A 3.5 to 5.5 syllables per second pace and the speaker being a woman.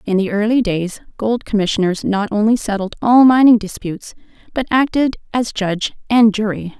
Yes: 5.2 syllables/s; female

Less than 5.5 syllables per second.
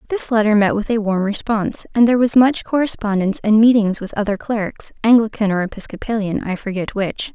No: 5.9 syllables/s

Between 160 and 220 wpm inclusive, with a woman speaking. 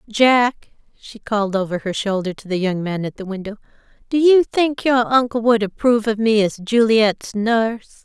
Yes: average, 185 wpm; female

